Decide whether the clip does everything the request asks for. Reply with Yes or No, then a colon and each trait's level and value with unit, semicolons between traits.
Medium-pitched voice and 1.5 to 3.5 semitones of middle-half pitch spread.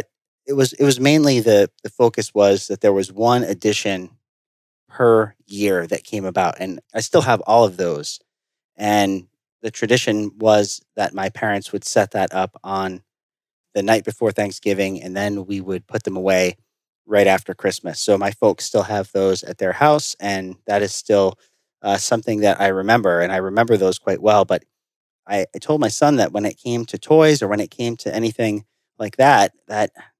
No: low, 105 Hz; average, 3.2 semitones